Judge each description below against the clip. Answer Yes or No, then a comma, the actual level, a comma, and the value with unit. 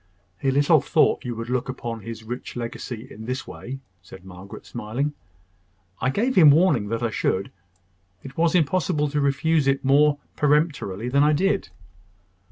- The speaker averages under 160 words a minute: No, average, 165 wpm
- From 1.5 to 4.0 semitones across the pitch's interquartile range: No, average, 4.5 semitones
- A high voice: No, low, 135 Hz